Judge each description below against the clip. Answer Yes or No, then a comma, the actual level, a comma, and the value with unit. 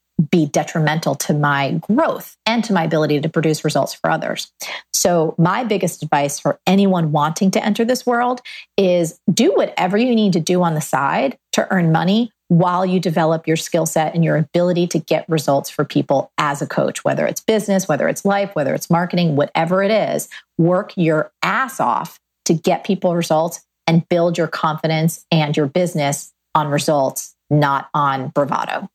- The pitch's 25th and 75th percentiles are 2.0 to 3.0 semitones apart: No, average, 3.4 semitones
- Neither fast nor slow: Yes, average, 180 wpm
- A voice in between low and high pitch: Yes, medium, 165 Hz